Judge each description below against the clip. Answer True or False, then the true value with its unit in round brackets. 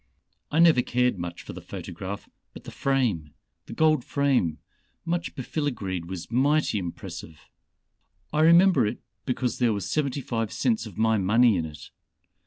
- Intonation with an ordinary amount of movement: False (7.4 semitones)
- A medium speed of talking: True (155 wpm)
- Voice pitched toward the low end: True (120 Hz)